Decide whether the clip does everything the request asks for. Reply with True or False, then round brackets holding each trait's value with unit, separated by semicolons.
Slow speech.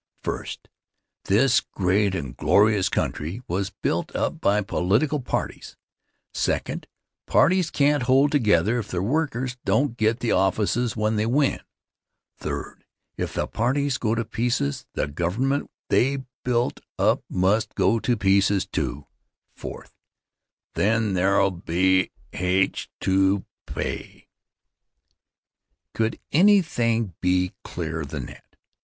True (120 wpm)